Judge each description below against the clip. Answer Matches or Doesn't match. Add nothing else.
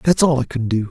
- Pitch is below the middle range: Matches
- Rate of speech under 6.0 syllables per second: Doesn't match